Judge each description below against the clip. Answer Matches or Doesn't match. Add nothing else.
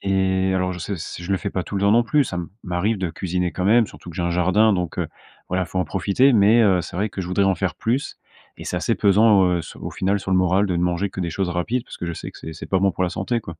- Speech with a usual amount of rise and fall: Doesn't match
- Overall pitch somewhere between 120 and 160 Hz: Doesn't match